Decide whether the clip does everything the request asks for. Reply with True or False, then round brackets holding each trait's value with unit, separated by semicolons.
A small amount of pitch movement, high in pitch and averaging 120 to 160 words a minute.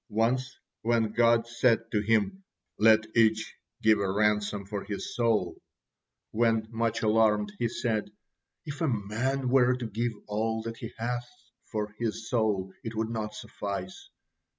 False (1.9 semitones; 110 Hz; 150 wpm)